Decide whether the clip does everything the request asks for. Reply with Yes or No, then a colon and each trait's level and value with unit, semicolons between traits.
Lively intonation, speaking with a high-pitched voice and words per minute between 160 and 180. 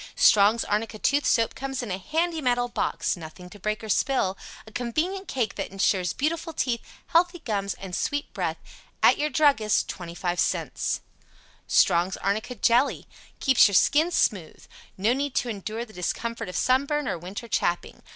Yes: wide, 6.1 semitones; high, 230 Hz; average, 170 wpm